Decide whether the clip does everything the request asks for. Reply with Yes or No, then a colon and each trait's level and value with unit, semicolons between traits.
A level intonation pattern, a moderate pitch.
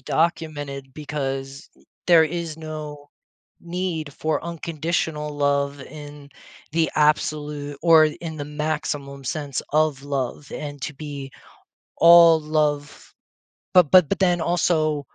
Yes: narrow, 2.0 semitones; medium, 150 Hz